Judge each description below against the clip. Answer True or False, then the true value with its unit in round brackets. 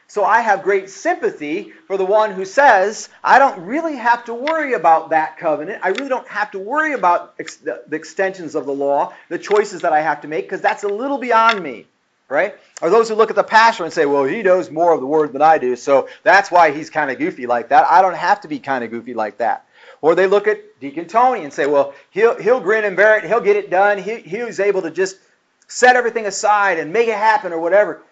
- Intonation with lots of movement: True (6.4 semitones)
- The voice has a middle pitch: False (200 Hz)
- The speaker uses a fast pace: True (255 wpm)